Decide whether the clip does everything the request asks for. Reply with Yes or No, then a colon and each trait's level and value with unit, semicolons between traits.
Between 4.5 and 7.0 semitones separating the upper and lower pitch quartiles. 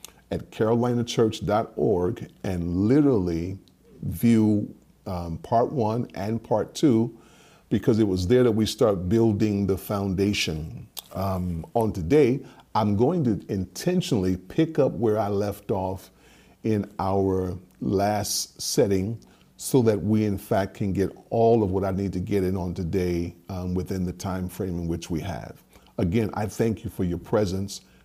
No: average, 3.2 semitones